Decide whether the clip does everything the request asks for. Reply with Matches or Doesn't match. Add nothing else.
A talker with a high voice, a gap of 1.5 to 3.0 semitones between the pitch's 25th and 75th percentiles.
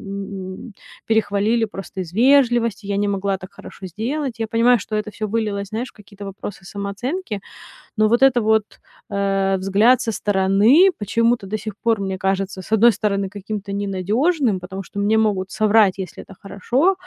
Matches